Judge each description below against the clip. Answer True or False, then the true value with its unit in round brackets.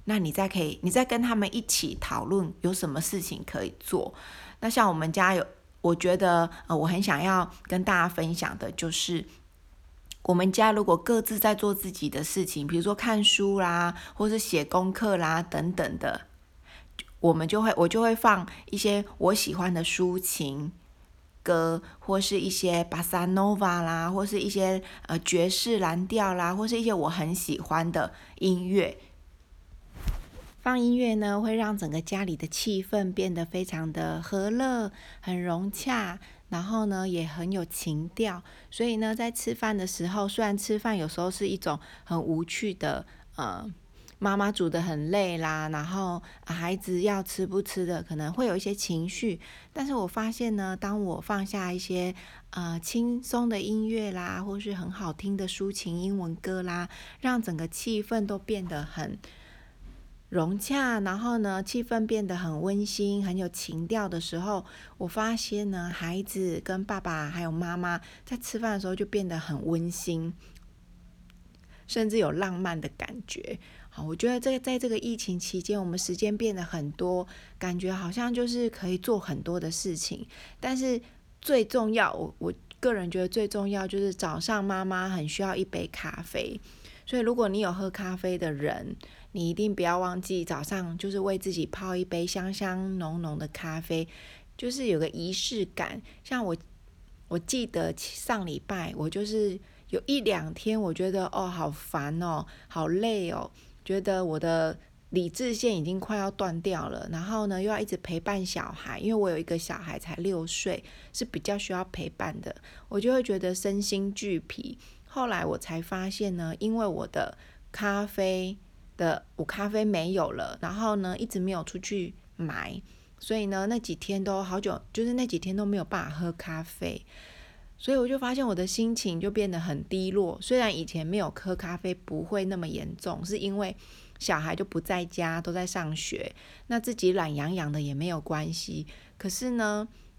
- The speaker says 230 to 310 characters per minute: True (250 characters per minute)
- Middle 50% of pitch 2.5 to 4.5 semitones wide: True (3.5 semitones)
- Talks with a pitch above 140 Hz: True (185 Hz)